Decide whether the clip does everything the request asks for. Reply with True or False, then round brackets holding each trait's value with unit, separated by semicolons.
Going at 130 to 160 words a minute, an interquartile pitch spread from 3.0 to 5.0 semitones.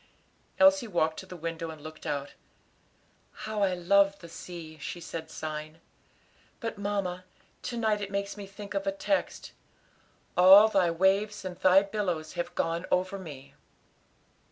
True (155 wpm; 3.3 semitones)